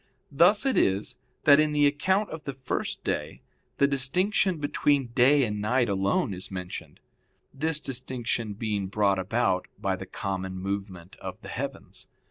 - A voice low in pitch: Yes, low, 125 Hz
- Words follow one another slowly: No, average, 155 wpm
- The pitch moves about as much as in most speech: No, wide, 6.8 semitones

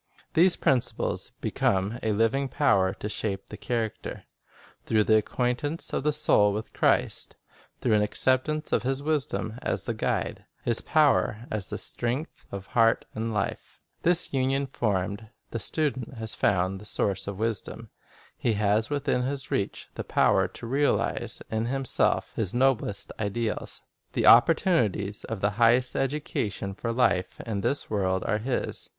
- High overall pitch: No, low, 115 Hz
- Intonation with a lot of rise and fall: No, average, 4.5 semitones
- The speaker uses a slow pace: No, average, 155 wpm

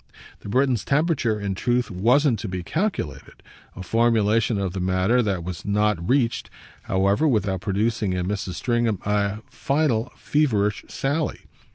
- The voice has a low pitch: Yes, low, 105 Hz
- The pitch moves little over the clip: No, average, 4.3 semitones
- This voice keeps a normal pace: Yes, average, 145 wpm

